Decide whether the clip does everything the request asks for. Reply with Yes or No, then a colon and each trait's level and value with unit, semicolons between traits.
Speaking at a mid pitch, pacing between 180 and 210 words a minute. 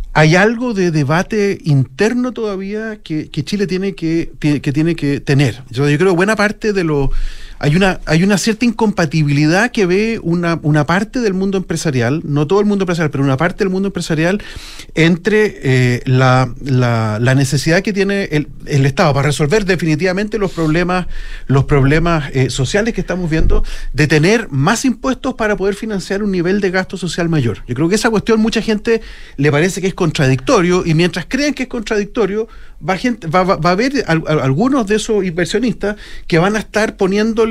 Yes: medium, 180 Hz; average, 185 wpm